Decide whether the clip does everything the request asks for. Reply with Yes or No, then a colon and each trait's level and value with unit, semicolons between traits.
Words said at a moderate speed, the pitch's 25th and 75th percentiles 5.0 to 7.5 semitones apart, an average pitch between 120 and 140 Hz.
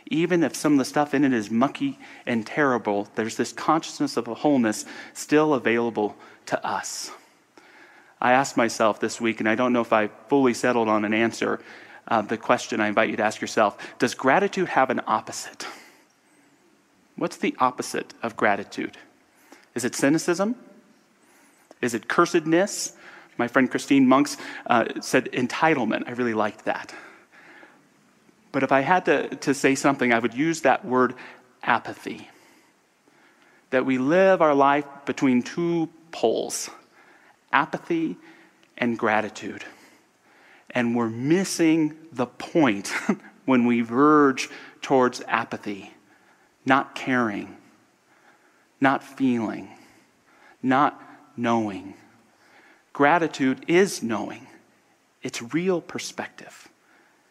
No: slow, 125 wpm; wide, 5.4 semitones; low, 135 Hz